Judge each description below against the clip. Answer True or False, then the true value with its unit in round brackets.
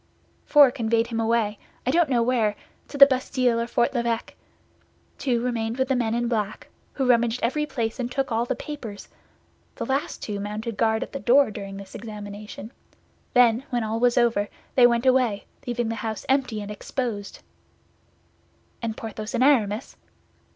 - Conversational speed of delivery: True (170 wpm)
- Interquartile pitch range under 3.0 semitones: True (2.5 semitones)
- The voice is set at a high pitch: True (235 Hz)